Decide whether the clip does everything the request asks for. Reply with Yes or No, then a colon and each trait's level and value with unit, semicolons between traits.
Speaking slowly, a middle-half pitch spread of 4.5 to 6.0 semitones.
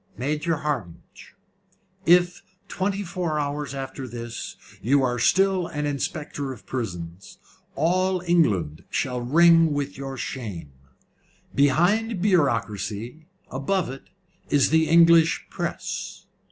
Yes: slow, 110 wpm; wide, 5.4 semitones